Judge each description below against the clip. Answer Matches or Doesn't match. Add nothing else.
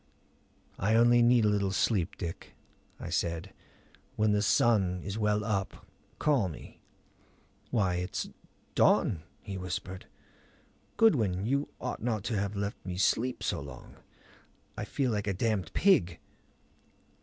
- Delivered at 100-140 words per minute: Matches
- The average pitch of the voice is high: Doesn't match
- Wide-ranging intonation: Doesn't match